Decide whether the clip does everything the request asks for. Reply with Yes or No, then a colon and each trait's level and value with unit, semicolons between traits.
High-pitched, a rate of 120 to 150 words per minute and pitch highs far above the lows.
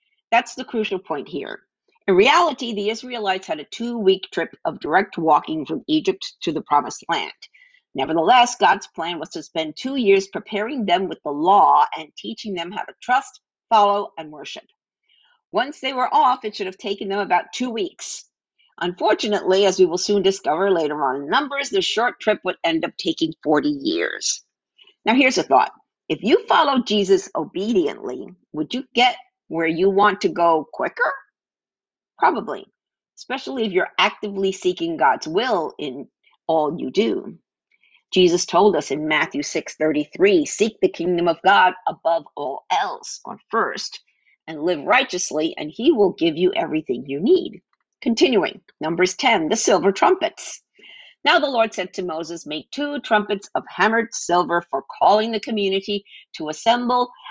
No: high, 215 Hz; average, 165 wpm; wide, 8.8 semitones